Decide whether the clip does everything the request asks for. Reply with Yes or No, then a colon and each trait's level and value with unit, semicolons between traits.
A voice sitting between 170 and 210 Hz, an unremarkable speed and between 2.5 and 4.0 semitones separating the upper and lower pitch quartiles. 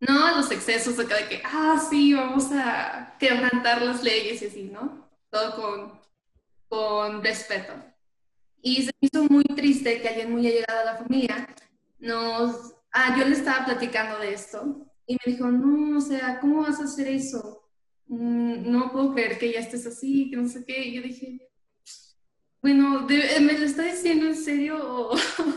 No: very high, 250 Hz; average, 175 wpm; average, 3.5 semitones